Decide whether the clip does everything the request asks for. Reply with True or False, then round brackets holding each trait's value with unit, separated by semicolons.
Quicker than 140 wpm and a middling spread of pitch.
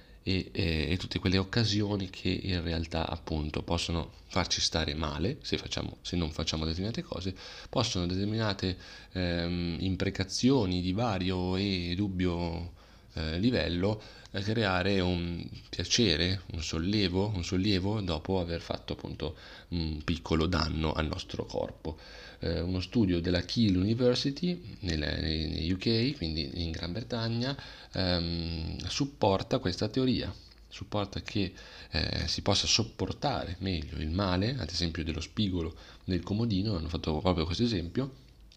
False (130 wpm; 3.5 semitones)